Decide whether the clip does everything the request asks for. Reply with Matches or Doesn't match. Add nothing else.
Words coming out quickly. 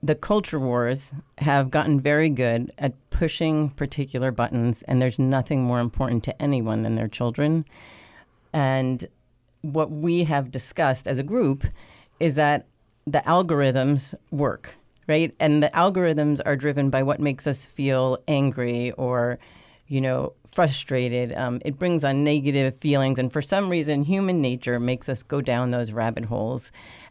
Doesn't match